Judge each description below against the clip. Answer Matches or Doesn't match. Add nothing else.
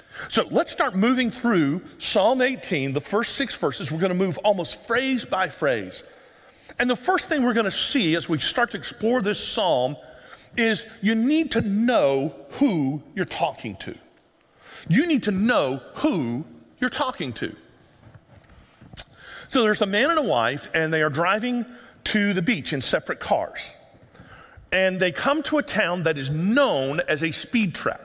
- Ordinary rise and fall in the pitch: Doesn't match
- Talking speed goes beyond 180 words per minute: Doesn't match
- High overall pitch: Matches